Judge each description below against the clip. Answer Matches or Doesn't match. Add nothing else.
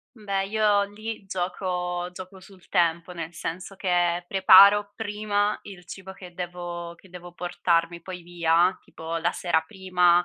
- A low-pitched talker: Doesn't match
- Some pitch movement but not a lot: Doesn't match